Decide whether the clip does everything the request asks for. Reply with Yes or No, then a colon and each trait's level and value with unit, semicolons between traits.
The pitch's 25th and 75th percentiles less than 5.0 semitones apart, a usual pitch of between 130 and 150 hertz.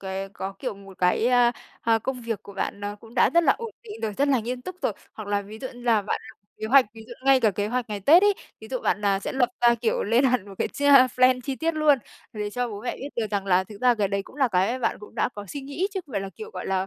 No: average, 4.3 semitones; high, 230 Hz